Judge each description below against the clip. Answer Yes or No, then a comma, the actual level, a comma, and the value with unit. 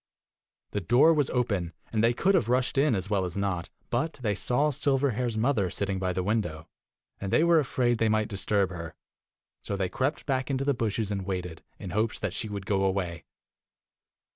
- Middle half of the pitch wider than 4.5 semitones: Yes, average, 5.1 semitones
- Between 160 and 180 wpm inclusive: No, average, 195 wpm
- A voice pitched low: Yes, low, 110 Hz